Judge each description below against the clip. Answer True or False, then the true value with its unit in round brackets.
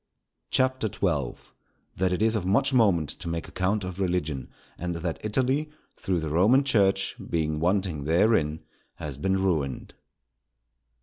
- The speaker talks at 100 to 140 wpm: True (135 wpm)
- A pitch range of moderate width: True (5.0 semitones)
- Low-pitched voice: True (90 Hz)